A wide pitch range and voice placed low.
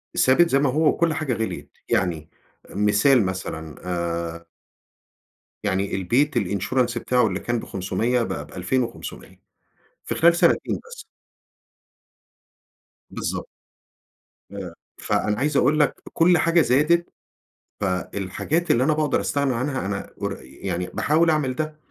Yes: wide, 8.1 semitones; low, 120 Hz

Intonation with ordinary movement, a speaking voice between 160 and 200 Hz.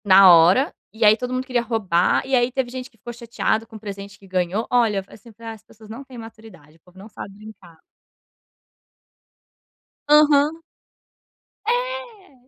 No: average, 4.5 semitones; high, 225 Hz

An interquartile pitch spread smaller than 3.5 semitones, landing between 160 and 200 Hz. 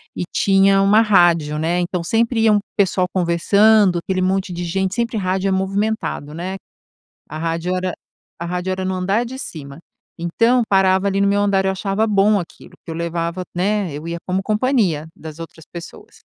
Yes: average, 2.9 semitones; high, 190 Hz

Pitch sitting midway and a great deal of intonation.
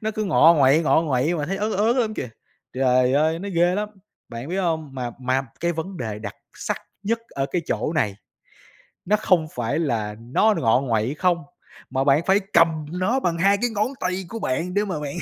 Yes: medium, 165 Hz; wide, 6.4 semitones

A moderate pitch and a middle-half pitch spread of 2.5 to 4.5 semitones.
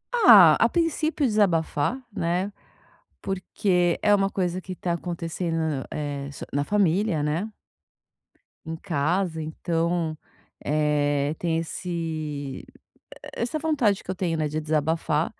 Yes: medium, 170 Hz; average, 4.1 semitones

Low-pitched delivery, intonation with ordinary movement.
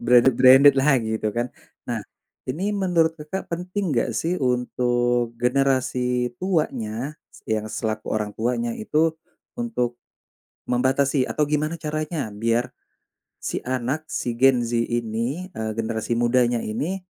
Yes: low, 125 Hz; average, 4.4 semitones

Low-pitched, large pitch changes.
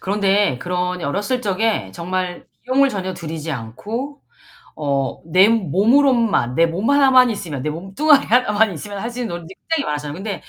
No: high, 195 Hz; wide, 6.1 semitones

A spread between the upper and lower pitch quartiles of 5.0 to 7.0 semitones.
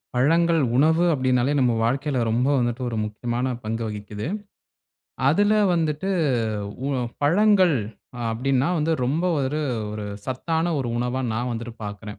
Yes: average, 5.3 semitones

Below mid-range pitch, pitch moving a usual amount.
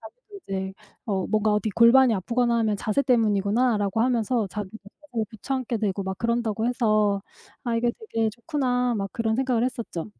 No: high, 225 Hz; average, 3.0 semitones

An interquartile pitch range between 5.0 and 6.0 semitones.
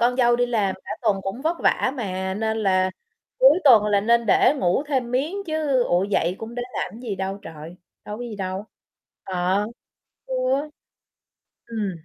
No: average, 4.4 semitones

